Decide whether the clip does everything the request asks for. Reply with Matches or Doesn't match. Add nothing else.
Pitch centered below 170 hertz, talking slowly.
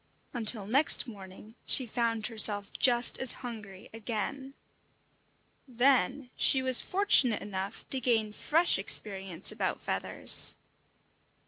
Doesn't match